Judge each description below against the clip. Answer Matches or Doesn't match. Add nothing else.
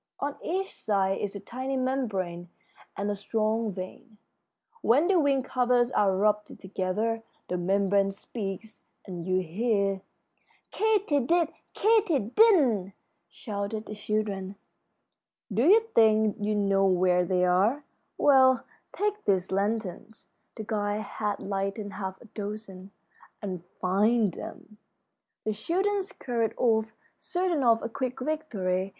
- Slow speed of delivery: Matches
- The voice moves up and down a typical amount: Matches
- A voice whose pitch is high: Matches